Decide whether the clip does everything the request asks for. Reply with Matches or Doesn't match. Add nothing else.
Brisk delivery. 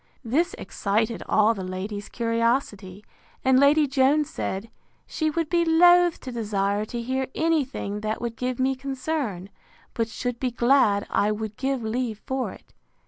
Doesn't match